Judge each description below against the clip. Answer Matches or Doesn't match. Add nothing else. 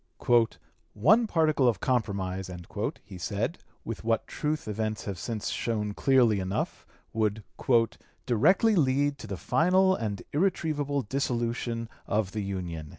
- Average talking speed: Doesn't match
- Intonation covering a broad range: Matches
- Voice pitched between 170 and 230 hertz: Doesn't match